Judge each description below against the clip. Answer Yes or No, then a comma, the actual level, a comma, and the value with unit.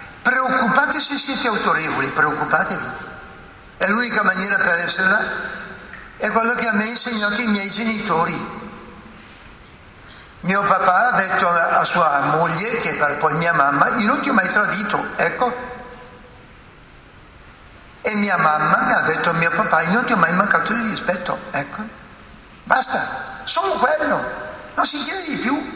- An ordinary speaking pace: Yes, average, 150 wpm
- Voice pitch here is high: Yes, high, 210 Hz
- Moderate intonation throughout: No, wide, 6.6 semitones